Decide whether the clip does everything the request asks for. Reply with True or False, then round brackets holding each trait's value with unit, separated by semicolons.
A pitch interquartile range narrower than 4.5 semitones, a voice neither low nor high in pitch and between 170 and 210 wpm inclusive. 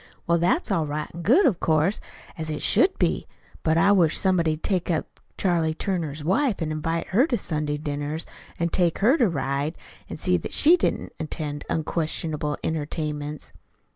True (3.3 semitones; 160 Hz; 175 wpm)